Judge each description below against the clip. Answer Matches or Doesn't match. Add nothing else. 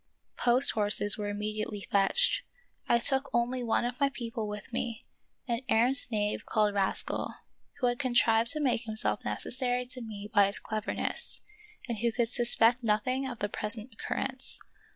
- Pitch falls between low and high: Doesn't match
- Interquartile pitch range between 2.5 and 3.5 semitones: Matches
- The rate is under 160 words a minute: Doesn't match